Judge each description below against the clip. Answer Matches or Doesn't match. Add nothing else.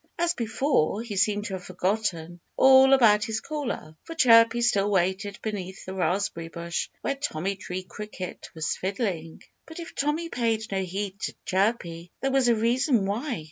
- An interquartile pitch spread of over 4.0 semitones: Matches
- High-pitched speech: Matches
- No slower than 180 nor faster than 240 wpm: Doesn't match